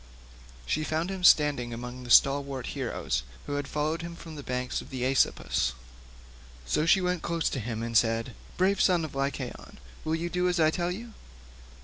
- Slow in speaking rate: No, average, 195 wpm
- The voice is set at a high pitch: No, medium, 150 Hz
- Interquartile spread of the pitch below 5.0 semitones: No, average, 5.3 semitones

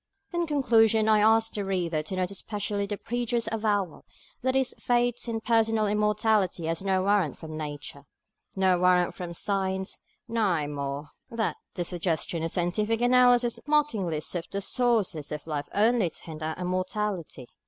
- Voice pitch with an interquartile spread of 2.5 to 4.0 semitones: No, average, 4.7 semitones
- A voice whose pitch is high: Yes, high, 200 Hz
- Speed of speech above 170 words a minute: No, average, 155 wpm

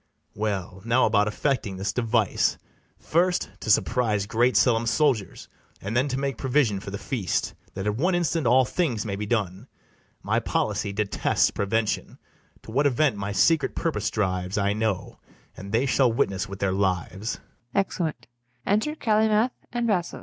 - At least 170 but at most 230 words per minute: No, average, 160 wpm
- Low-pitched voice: Yes, low, 115 Hz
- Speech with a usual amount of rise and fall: No, wide, 6.0 semitones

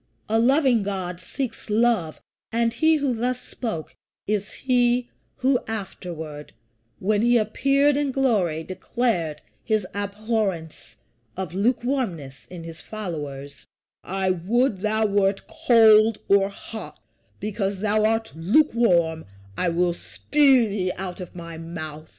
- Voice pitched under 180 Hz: No, high, 205 Hz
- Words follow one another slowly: Yes, slow, 125 wpm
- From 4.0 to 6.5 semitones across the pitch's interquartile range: Yes, average, 5.3 semitones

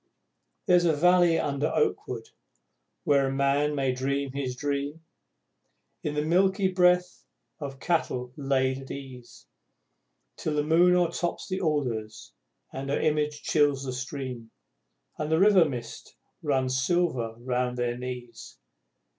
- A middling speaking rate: No, slow, 130 wpm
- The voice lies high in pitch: No, medium, 140 Hz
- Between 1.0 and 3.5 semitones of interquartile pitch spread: No, average, 4.1 semitones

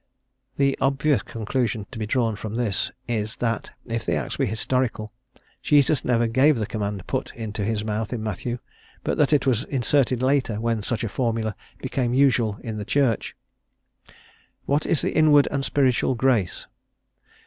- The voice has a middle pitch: No, low, 120 Hz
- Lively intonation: No, average, 3.6 semitones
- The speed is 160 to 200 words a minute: Yes, average, 165 wpm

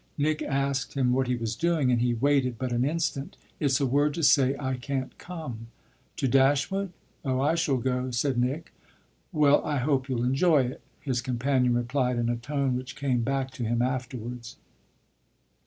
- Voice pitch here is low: Yes, low, 130 Hz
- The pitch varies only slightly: Yes, narrow, 2.3 semitones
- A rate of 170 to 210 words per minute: Yes, average, 180 wpm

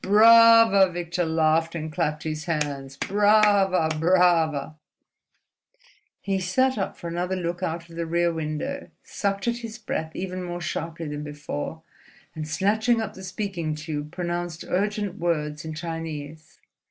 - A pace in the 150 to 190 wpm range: No, average, 140 wpm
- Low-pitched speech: No, medium, 175 Hz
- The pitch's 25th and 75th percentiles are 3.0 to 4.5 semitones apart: Yes, average, 3.8 semitones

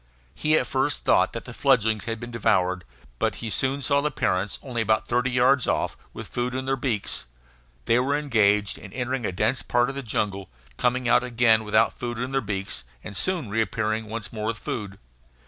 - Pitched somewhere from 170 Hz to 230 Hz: No, low, 115 Hz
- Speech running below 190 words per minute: No, average, 200 wpm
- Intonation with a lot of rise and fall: No, average, 3.5 semitones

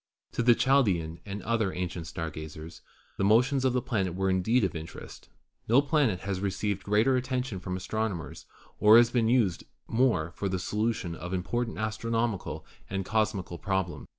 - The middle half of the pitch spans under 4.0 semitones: No, average, 4.3 semitones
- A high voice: No, low, 105 Hz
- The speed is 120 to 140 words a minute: No, average, 175 wpm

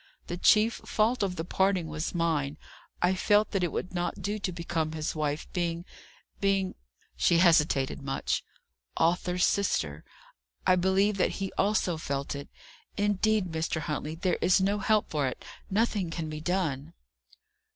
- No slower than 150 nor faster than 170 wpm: Yes, average, 160 wpm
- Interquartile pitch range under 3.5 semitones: No, average, 3.8 semitones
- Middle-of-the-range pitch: Yes, medium, 175 Hz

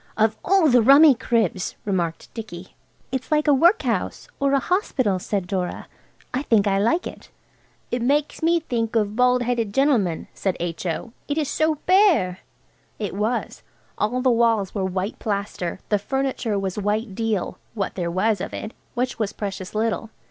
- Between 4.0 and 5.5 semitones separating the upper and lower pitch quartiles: Yes, average, 5.1 semitones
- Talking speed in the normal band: Yes, average, 165 wpm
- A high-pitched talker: Yes, high, 225 Hz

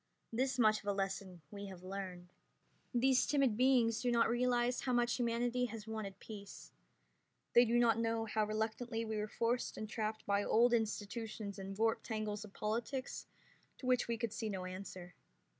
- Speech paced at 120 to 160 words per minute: No, average, 175 wpm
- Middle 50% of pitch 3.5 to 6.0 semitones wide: No, average, 2.9 semitones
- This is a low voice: No, high, 220 Hz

